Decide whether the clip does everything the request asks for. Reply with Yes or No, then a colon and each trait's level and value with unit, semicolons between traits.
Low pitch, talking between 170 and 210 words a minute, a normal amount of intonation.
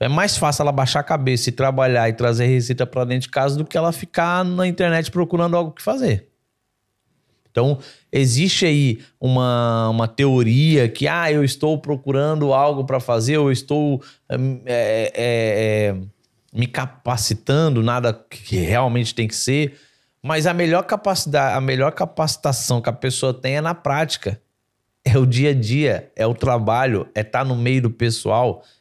Yes: low, 130 Hz; average, 175 wpm; average, 3.7 semitones